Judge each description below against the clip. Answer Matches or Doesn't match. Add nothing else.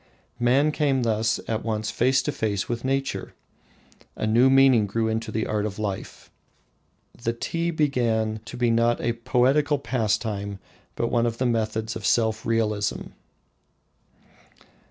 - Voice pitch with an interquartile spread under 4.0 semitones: Matches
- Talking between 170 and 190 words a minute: Doesn't match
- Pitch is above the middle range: Doesn't match